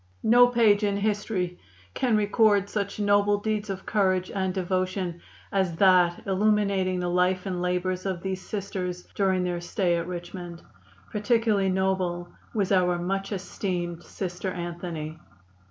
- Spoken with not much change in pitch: Yes, narrow, 2.3 semitones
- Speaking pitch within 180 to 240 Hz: Yes, high, 190 Hz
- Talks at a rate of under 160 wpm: Yes, average, 140 wpm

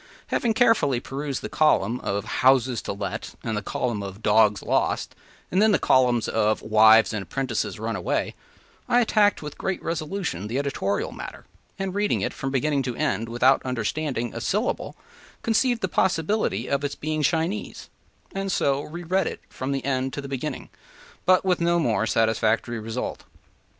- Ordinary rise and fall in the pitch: No, wide, 7.3 semitones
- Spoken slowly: No, average, 170 wpm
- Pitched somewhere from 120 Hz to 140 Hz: Yes, low, 135 Hz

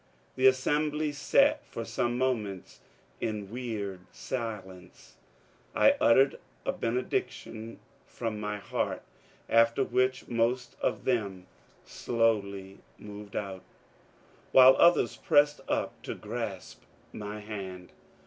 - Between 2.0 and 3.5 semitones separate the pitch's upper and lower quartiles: No, average, 4.0 semitones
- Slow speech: Yes, slow, 105 wpm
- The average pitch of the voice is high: No, low, 115 Hz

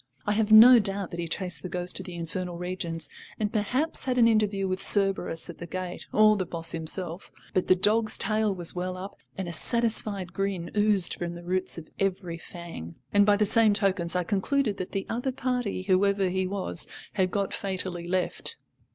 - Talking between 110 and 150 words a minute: No, average, 200 wpm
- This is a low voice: No, high, 190 Hz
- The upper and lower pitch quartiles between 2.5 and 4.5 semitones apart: Yes, average, 2.8 semitones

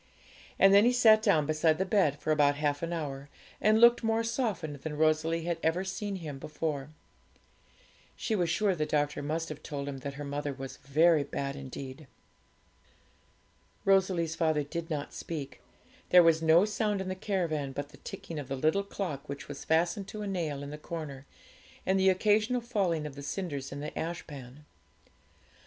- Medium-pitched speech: Yes, medium, 160 Hz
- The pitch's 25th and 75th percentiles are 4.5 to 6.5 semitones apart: Yes, average, 4.8 semitones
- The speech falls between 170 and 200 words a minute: Yes, average, 180 wpm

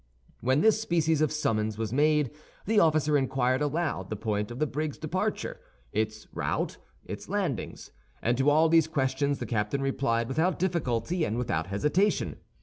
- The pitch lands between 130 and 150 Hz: Yes, medium, 140 Hz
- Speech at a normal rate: Yes, average, 160 wpm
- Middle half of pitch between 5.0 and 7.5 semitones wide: Yes, wide, 5.4 semitones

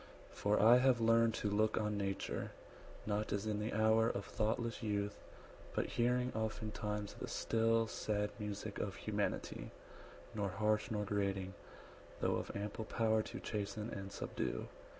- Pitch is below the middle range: Yes, low, 105 Hz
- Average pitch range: No, narrow, 1.6 semitones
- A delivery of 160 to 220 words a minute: No, average, 150 wpm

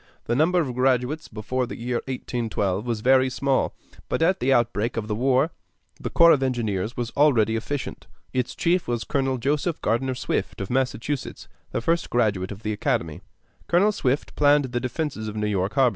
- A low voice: Yes, low, 125 Hz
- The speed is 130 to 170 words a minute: No, average, 185 wpm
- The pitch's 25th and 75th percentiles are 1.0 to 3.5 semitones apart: No, average, 4.0 semitones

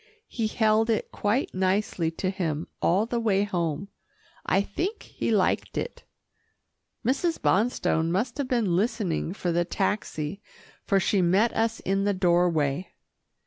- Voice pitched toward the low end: No, high, 195 Hz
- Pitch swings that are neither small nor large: Yes, average, 4.3 semitones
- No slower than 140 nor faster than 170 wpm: Yes, average, 145 wpm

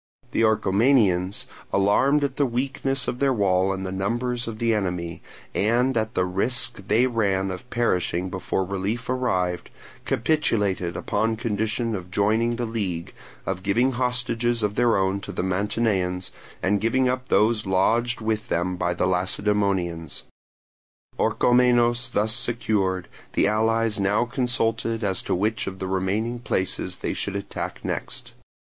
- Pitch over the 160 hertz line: No, low, 105 Hz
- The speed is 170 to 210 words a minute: No, average, 145 wpm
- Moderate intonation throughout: Yes, average, 4.0 semitones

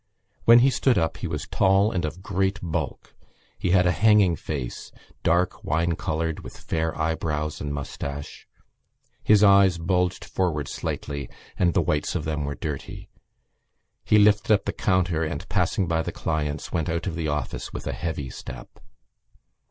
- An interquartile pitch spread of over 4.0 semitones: No, average, 3.7 semitones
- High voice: No, very low, 80 Hz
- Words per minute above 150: Yes, average, 165 wpm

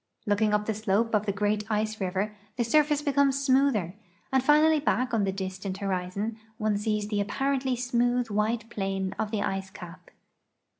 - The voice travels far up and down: No, average, 3.9 semitones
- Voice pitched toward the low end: No, high, 215 Hz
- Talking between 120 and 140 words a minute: No, average, 170 wpm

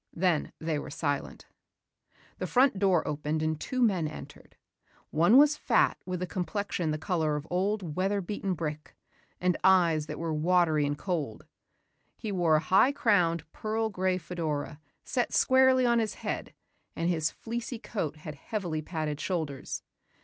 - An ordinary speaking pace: Yes, average, 155 wpm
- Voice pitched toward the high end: No, medium, 175 Hz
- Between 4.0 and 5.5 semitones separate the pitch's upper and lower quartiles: Yes, average, 4.7 semitones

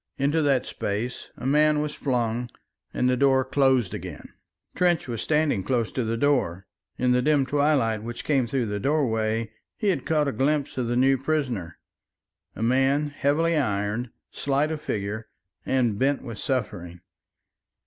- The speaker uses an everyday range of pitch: Yes, average, 4.0 semitones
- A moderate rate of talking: Yes, average, 160 wpm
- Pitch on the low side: Yes, low, 130 Hz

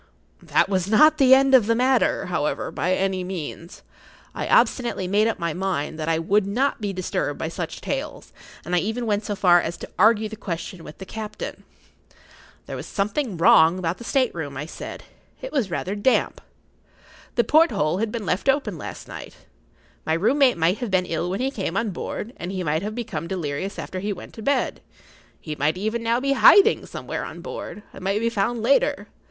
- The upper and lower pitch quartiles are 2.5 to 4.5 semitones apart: No, average, 4.9 semitones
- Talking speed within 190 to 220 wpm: Yes, fast, 205 wpm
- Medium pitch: No, high, 200 Hz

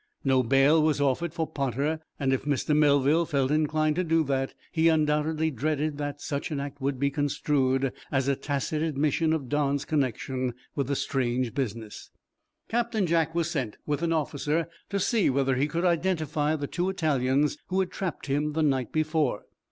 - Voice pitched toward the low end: No, medium, 145 Hz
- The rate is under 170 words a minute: No, average, 175 wpm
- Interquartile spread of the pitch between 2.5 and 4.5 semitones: Yes, average, 2.8 semitones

